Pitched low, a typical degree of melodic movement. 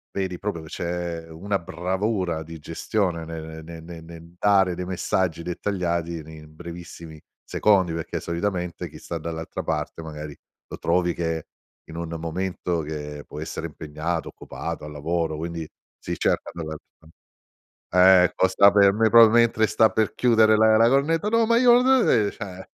Yes: very low, 85 Hz; average, 3.8 semitones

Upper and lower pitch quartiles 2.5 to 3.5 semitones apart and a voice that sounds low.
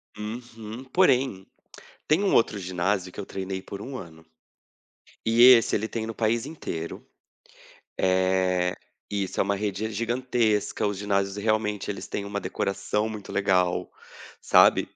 Yes: average, 3.1 semitones; low, 105 Hz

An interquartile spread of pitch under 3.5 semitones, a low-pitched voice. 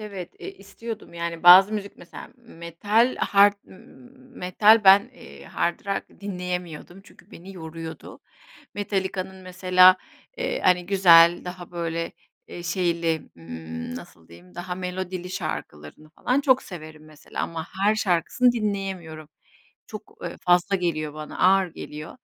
No: average, 2.9 semitones; medium, 180 Hz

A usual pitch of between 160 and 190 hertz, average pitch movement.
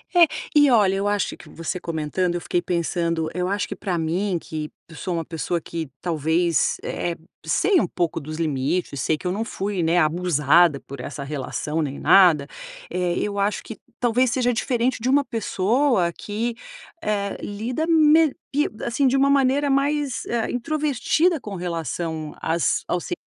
No: medium, 185 Hz; wide, 6.8 semitones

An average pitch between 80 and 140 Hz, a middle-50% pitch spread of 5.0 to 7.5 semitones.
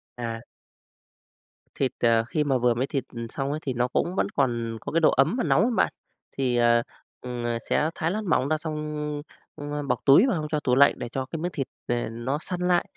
No: low, 135 Hz; average, 4.4 semitones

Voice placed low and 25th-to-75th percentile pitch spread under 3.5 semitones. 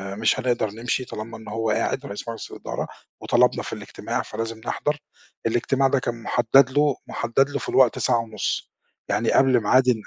Yes: low, 120 Hz; average, 2.8 semitones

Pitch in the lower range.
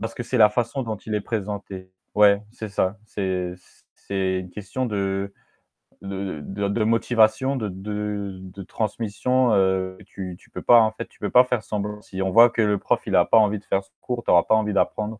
Yes: low, 105 Hz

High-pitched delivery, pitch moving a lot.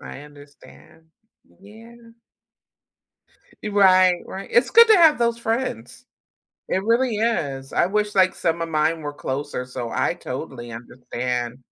No: medium, 170 Hz; wide, 8.7 semitones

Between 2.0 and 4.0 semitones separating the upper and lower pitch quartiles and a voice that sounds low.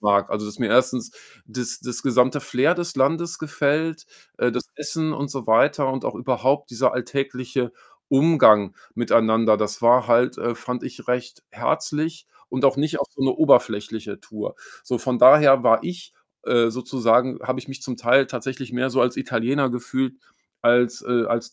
Yes: narrow, 2.6 semitones; low, 125 Hz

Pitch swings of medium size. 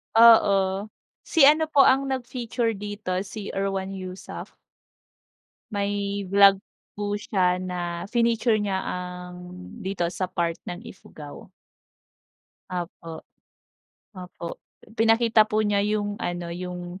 Yes: average, 3.2 semitones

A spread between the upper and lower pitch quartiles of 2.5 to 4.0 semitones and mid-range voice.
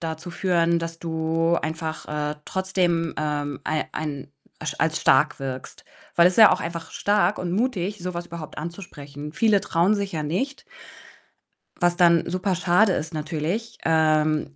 Yes: average, 2.9 semitones; medium, 165 Hz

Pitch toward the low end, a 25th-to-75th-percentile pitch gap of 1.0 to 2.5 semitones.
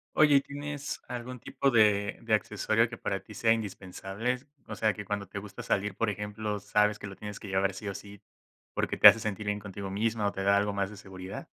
Yes: low, 105 Hz; narrow, 2.1 semitones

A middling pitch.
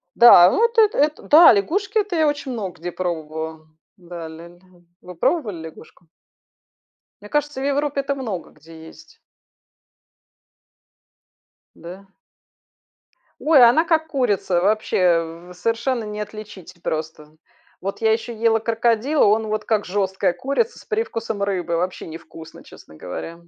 No: high, 210 Hz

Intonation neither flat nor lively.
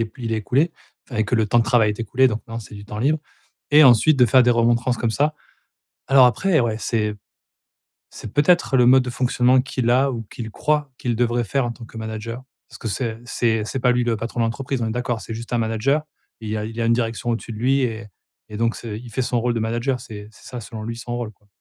No: narrow, 2.2 semitones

